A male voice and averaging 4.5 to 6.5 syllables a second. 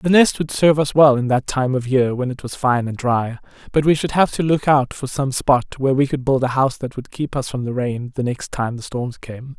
Yes: male; 5.4 syllables/s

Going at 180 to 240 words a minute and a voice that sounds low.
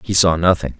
Yes: fast, 230 wpm; very low, 85 Hz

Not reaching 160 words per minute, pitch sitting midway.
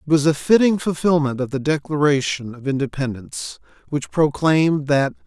Yes: average, 150 wpm; medium, 145 Hz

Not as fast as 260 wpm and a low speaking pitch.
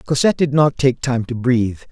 Yes: fast, 220 wpm; low, 130 Hz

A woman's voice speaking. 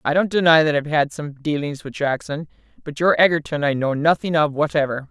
Yes: female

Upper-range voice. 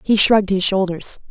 Yes: high, 195 Hz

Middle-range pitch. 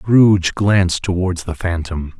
No: very low, 90 Hz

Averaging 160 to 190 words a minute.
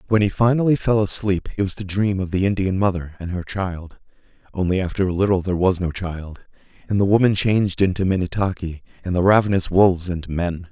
No: average, 200 wpm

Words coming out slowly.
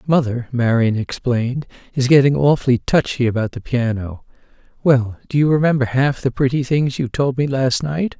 No: average, 170 wpm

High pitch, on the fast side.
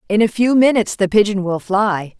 Yes: high, 205 Hz; fast, 220 wpm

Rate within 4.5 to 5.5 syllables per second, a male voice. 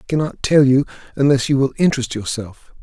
No: 6.1 syllables/s; male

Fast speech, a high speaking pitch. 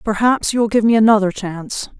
Yes: fast, 210 wpm; high, 215 Hz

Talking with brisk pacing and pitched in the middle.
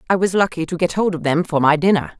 Yes: fast, 300 wpm; medium, 170 Hz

